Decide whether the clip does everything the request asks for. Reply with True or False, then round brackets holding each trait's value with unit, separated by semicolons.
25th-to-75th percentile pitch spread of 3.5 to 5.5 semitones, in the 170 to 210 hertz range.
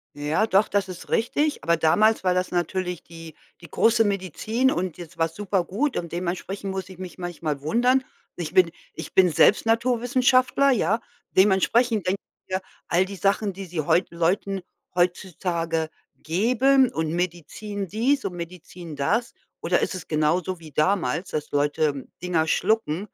True (4.2 semitones; 185 Hz)